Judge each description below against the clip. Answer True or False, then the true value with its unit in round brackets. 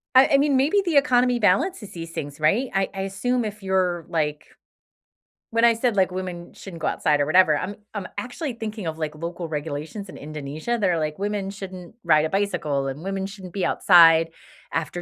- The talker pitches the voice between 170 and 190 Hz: True (185 Hz)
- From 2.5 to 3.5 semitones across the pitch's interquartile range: False (5.1 semitones)